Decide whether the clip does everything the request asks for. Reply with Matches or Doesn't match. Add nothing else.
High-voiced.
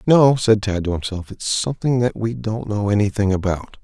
Doesn't match